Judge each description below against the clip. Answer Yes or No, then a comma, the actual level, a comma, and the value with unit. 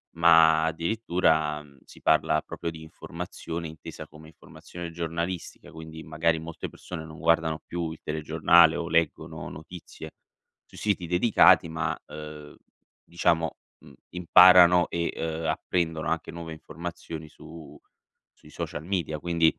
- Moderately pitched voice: No, very low, 80 Hz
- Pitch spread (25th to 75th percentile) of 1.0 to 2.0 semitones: Yes, narrow, 1.4 semitones